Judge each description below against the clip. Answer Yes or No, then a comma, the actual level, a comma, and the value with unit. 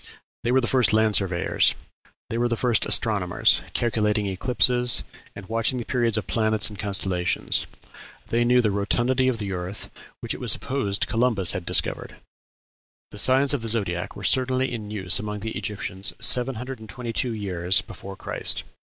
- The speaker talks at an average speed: Yes, average, 165 wpm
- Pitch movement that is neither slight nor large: Yes, average, 3.6 semitones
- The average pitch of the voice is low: Yes, low, 110 Hz